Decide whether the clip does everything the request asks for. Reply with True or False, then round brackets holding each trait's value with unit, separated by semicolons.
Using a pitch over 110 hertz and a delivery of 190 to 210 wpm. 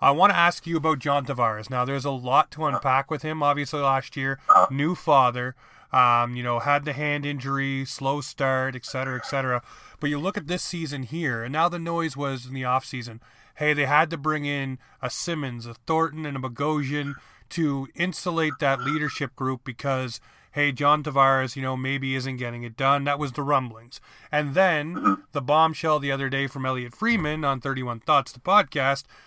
True (140 Hz; 200 wpm)